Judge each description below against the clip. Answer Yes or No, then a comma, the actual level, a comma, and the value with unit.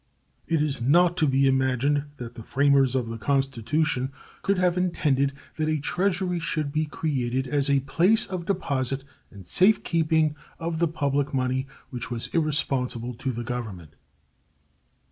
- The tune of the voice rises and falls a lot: No, average, 3.9 semitones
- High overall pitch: No, medium, 140 Hz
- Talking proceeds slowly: No, average, 155 wpm